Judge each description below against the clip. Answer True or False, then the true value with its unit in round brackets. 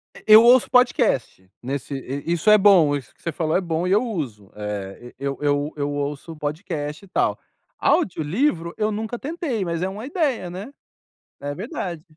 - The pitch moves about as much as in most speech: False (6.8 semitones)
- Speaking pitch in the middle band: True (170 Hz)